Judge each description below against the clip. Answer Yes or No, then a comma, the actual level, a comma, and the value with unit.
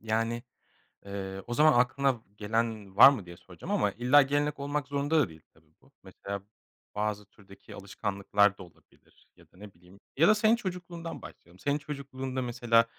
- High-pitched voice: No, low, 115 Hz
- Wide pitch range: Yes, wide, 6.2 semitones